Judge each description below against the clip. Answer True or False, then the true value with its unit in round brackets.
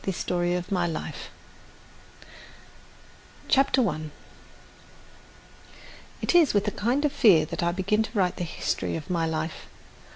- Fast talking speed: False (140 wpm)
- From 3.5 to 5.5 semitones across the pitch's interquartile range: True (4.5 semitones)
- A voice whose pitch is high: False (180 Hz)